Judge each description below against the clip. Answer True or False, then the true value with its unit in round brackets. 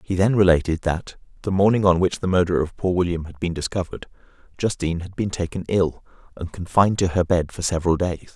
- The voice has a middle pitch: False (90 Hz)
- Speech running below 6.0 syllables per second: False (6.1 syllables/s)